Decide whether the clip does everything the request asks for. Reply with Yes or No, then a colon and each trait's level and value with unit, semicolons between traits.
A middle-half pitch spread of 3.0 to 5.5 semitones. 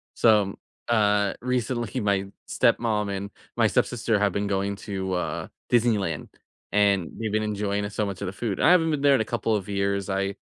No: narrow, 2.4 semitones